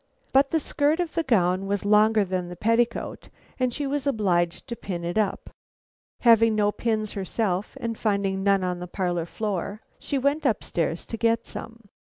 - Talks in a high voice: Yes, high, 215 Hz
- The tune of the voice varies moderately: Yes, average, 4.0 semitones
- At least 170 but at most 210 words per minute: Yes, average, 185 wpm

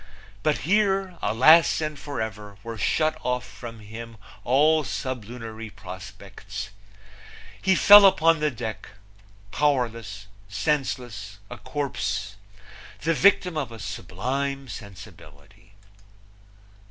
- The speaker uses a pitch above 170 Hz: No, low, 125 Hz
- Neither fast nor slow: No, slow, 100 wpm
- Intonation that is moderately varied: No, wide, 6.3 semitones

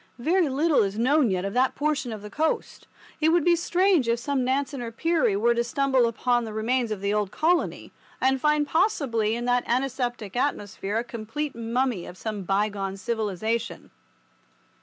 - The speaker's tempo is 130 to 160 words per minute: No, average, 180 wpm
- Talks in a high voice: Yes, high, 240 Hz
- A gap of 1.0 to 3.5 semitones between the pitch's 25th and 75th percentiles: No, average, 4.7 semitones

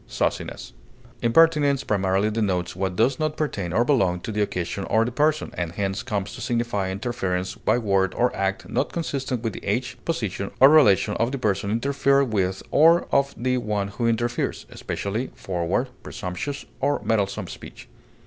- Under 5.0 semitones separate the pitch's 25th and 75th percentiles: No, average, 5.3 semitones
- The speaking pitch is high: No, low, 110 Hz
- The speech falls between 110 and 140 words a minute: No, average, 165 wpm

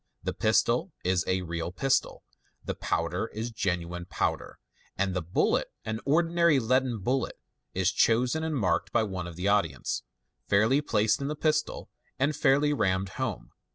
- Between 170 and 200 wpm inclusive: No, average, 160 wpm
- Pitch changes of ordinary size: No, wide, 6.9 semitones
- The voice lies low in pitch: Yes, low, 110 Hz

